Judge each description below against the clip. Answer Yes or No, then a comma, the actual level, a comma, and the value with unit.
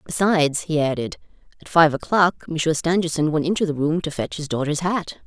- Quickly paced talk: No, average, 195 wpm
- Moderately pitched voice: Yes, medium, 160 Hz